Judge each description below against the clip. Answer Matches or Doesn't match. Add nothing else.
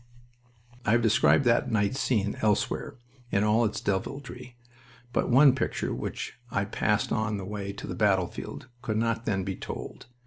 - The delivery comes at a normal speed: Matches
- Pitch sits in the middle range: Doesn't match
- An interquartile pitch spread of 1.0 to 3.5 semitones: Matches